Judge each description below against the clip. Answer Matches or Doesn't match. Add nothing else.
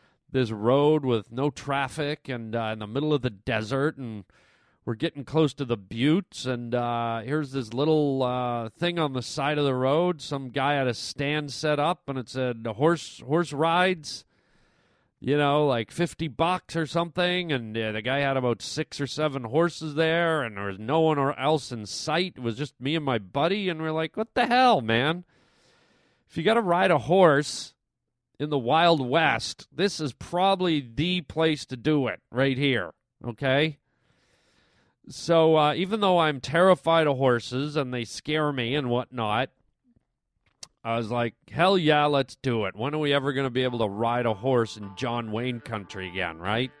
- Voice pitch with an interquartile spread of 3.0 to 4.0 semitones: Doesn't match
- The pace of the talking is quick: Doesn't match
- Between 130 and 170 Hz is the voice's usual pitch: Matches